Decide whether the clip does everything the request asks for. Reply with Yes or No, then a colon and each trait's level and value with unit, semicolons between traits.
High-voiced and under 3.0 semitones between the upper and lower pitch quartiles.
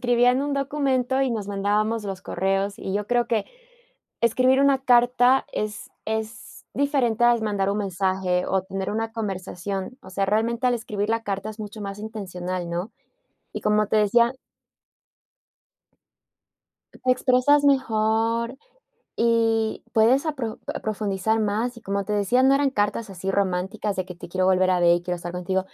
No: high, 215 Hz; average, 3.7 semitones